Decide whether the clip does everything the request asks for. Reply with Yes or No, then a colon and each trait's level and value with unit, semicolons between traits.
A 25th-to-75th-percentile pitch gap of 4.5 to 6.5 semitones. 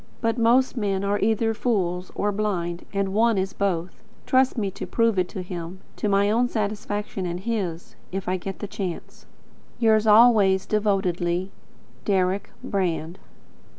No: average, 2.9 semitones